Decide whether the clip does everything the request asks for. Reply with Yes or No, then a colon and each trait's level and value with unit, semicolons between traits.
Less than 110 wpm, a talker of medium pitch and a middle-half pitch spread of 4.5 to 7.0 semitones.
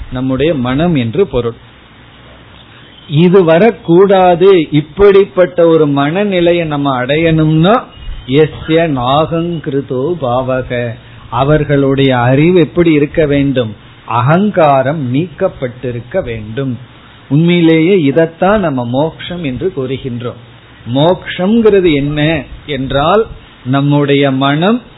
Yes: slow, 75 wpm; medium, 145 Hz; average, 4.9 semitones